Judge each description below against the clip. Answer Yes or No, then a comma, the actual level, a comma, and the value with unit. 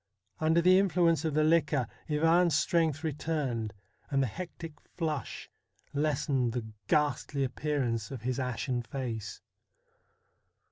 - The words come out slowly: Yes, slow, 120 wpm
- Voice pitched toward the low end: No, medium, 150 Hz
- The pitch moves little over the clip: No, average, 4.1 semitones